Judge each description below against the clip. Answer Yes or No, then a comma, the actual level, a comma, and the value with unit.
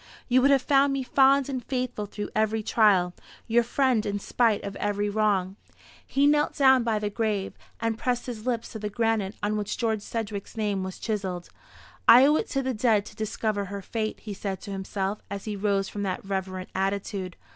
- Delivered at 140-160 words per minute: No, average, 200 wpm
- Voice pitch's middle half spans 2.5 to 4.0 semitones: Yes, average, 3.2 semitones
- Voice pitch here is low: No, high, 215 Hz